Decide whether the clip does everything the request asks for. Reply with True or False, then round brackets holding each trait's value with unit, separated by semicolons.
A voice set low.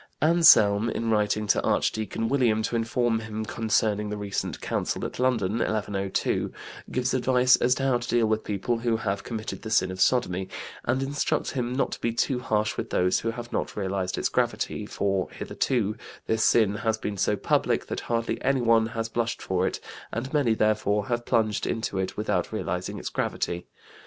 True (110 Hz)